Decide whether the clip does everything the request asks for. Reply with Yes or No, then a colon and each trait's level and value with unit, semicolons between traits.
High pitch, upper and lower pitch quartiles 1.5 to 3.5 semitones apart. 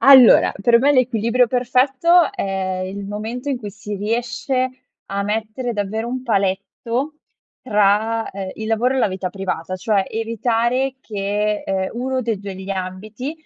No: high, 220 Hz; average, 4.1 semitones